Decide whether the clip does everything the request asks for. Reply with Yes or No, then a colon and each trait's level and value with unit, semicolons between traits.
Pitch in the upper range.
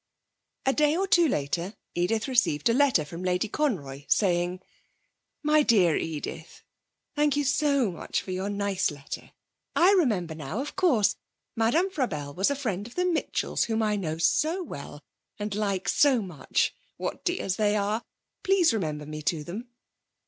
Yes: high, 210 Hz